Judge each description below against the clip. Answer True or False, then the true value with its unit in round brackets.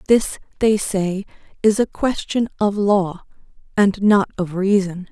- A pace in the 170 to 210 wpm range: False (140 wpm)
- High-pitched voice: True (200 Hz)